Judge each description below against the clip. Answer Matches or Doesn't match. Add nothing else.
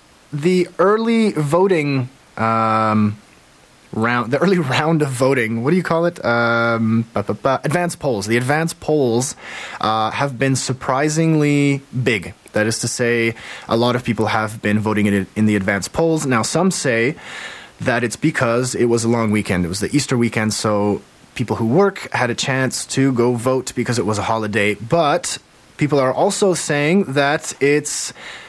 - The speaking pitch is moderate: Doesn't match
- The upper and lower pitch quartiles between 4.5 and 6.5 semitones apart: Matches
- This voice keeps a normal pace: Matches